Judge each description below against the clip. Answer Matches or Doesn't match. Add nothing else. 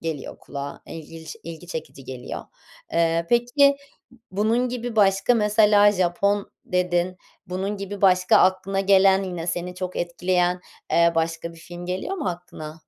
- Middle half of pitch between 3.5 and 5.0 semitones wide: Doesn't match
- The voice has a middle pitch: Matches